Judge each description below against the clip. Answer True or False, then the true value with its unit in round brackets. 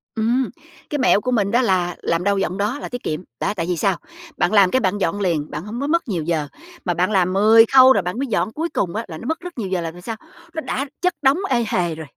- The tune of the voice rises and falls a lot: True (6.0 semitones)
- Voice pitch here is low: False (205 Hz)